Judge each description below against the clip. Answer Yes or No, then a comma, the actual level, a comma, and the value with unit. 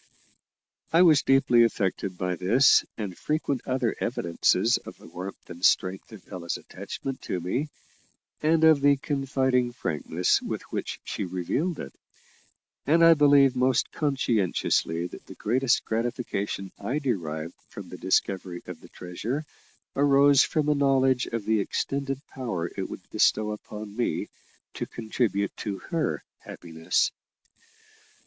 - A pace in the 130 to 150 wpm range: Yes, average, 140 wpm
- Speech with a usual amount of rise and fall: No, wide, 6.7 semitones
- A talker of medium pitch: No, low, 120 Hz